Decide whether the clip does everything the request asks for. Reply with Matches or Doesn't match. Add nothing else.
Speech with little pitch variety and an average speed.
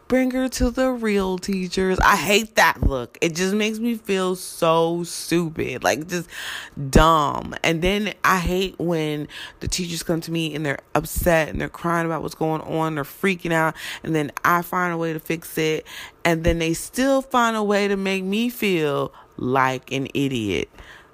Doesn't match